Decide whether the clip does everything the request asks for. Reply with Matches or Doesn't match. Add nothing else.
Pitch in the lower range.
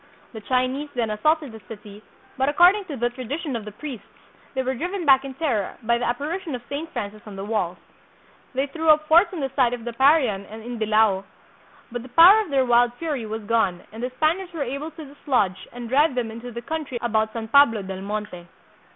Doesn't match